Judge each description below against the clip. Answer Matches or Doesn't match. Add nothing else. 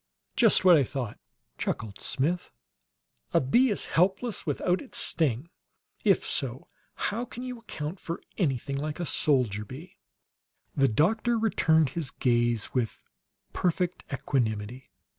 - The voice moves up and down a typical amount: Doesn't match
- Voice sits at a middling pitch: Matches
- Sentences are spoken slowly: Matches